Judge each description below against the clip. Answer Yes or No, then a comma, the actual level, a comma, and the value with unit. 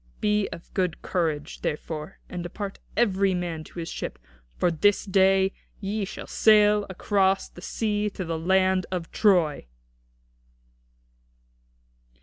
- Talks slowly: Yes, slow, 130 wpm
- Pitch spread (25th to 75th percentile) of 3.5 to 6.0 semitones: No, average, 3.0 semitones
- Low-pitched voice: No, high, 190 Hz